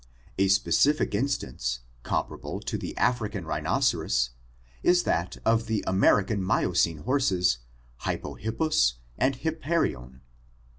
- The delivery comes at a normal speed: No, slow, 105 wpm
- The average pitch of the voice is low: Yes, low, 100 Hz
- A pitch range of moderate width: No, wide, 8.7 semitones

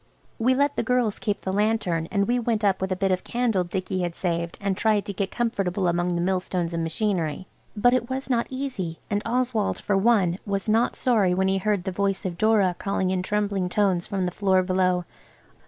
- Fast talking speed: Yes, fast, 215 wpm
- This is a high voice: Yes, high, 195 Hz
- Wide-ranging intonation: No, average, 3.3 semitones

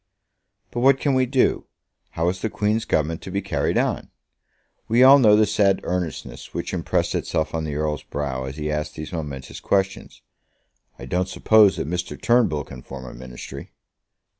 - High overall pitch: No, very low, 90 Hz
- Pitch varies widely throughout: Yes, wide, 6.2 semitones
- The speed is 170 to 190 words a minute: Yes, average, 180 wpm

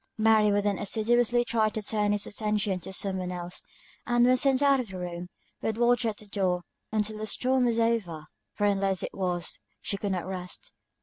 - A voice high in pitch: Yes, high, 210 Hz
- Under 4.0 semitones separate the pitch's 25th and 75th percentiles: Yes, average, 3.5 semitones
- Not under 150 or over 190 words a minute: No, average, 200 wpm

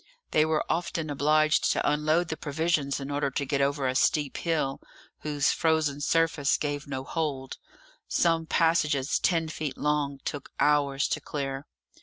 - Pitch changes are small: Yes, narrow, 2.2 semitones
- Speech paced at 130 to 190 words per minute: Yes, average, 155 wpm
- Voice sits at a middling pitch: Yes, medium, 150 Hz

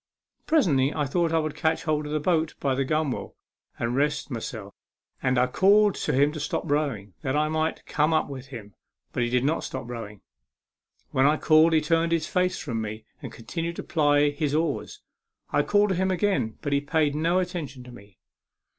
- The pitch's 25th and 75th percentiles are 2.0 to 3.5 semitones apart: No, average, 3.9 semitones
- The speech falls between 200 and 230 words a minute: Yes, fast, 205 wpm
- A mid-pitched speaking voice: Yes, medium, 150 Hz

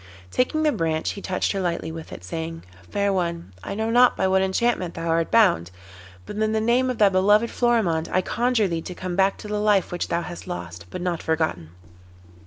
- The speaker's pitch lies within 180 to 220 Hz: Yes, medium, 185 Hz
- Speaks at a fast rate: Yes, fast, 215 wpm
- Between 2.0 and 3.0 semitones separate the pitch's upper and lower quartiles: No, average, 4.7 semitones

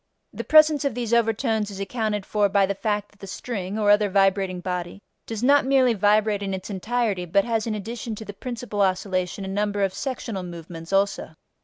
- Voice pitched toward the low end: No, high, 205 Hz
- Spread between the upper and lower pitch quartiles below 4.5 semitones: Yes, average, 2.8 semitones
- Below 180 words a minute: No, average, 200 wpm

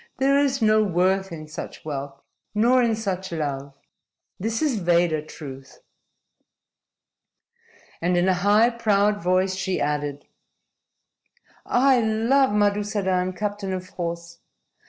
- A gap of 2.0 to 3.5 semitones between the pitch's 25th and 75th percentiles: No, average, 4.3 semitones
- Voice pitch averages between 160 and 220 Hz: Yes, high, 190 Hz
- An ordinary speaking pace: No, slow, 115 wpm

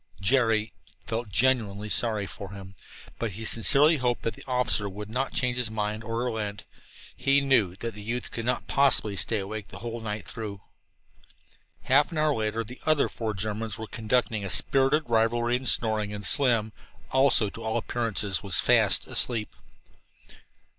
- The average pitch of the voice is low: Yes, low, 115 Hz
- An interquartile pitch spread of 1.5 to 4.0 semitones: Yes, average, 2.9 semitones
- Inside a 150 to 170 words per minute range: Yes, average, 165 wpm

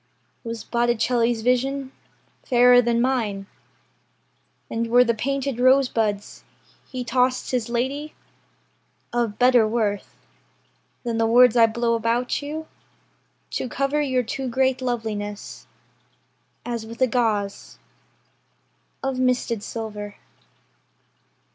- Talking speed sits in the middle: No, slow, 105 wpm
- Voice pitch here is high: Yes, high, 240 Hz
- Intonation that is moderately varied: No, narrow, 2.2 semitones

